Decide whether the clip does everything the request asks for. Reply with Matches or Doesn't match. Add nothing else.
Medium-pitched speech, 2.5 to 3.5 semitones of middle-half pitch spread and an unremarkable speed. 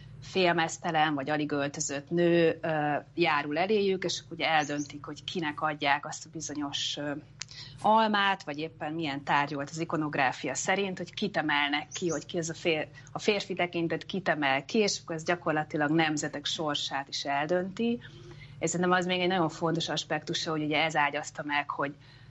Doesn't match